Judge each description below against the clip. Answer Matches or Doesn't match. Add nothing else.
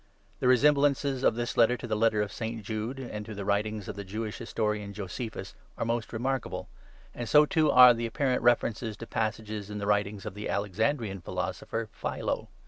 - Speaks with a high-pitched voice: Doesn't match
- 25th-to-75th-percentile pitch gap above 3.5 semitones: Doesn't match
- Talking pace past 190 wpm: Matches